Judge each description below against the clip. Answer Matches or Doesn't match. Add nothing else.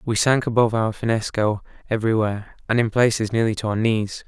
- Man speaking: Matches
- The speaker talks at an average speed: Matches